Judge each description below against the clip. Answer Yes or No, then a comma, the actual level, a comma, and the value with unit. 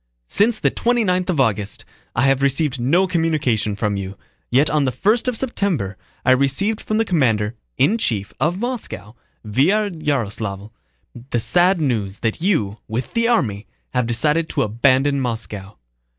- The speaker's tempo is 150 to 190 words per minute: Yes, average, 160 wpm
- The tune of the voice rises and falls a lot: Yes, wide, 8.7 semitones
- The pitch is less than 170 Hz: Yes, low, 135 Hz